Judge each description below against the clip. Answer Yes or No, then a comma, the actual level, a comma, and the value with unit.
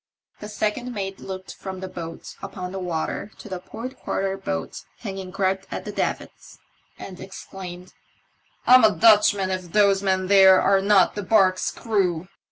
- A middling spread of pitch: No, narrow, 1.7 semitones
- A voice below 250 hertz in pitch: Yes, high, 190 Hz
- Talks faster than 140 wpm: Yes, average, 170 wpm